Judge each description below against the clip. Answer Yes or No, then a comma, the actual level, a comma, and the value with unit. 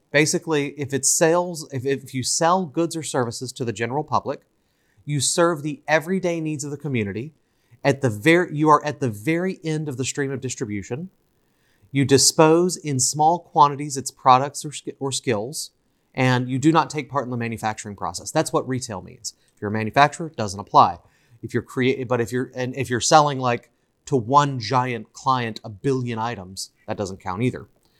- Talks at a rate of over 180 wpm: Yes, average, 195 wpm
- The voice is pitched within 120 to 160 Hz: Yes, low, 135 Hz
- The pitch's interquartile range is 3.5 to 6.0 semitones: Yes, average, 3.9 semitones